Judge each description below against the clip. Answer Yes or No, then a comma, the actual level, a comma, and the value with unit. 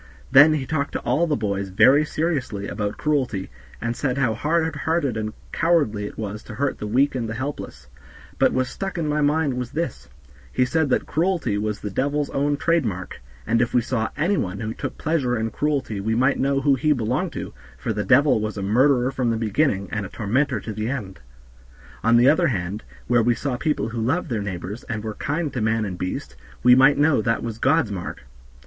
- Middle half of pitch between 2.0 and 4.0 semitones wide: No, average, 5.2 semitones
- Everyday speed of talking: No, fast, 220 wpm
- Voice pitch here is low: Yes, low, 125 Hz